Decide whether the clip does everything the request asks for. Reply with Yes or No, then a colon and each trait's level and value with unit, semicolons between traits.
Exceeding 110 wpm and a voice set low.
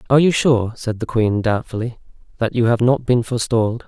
Yes: average, 200 wpm; low, 120 Hz